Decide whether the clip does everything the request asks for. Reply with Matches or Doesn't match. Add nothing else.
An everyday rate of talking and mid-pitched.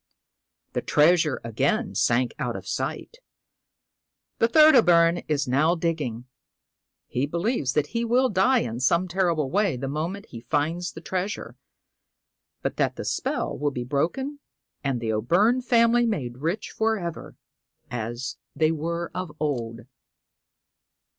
Matches